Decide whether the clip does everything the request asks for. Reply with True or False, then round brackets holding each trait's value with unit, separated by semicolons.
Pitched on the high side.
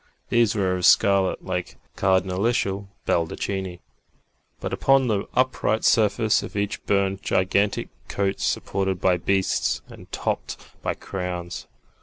False (95 Hz)